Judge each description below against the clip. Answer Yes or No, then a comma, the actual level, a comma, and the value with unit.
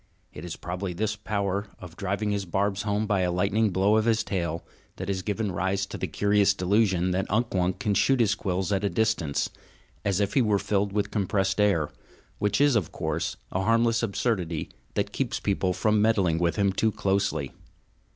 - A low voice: Yes, low, 100 Hz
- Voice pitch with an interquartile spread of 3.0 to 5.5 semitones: No, narrow, 2.4 semitones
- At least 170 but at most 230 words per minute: Yes, average, 195 wpm